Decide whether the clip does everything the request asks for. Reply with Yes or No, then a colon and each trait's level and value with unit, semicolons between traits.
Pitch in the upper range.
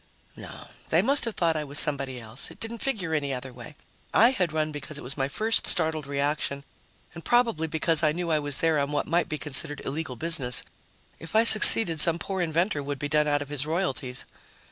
No: medium, 155 Hz